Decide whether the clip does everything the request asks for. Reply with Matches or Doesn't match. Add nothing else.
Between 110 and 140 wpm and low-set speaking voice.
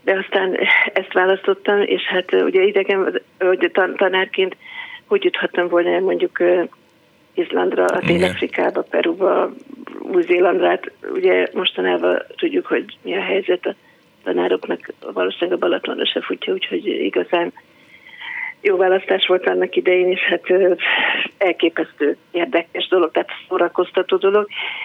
Doesn't match